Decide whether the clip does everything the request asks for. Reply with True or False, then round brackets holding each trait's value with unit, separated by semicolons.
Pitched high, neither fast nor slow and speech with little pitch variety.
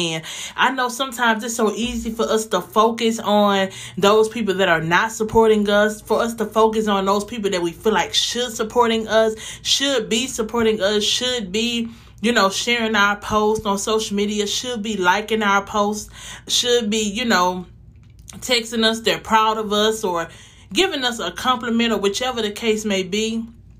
True (220 Hz; 185 wpm; 2.2 semitones)